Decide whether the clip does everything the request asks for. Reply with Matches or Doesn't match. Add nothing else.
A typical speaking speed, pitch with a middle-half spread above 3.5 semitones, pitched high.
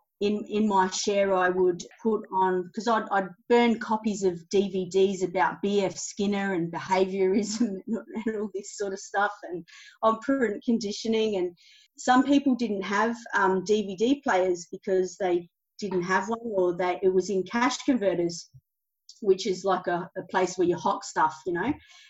Doesn't match